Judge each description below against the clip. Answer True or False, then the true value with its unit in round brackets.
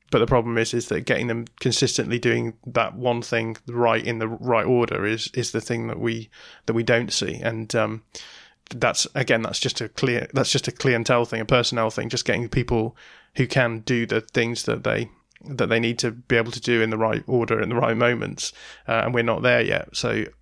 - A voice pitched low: True (120 Hz)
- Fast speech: True (225 wpm)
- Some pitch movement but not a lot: False (1.4 semitones)